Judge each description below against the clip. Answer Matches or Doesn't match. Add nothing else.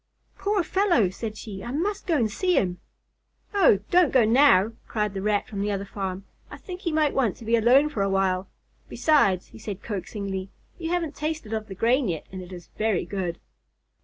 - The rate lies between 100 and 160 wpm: Doesn't match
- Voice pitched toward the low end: Doesn't match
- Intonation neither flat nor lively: Doesn't match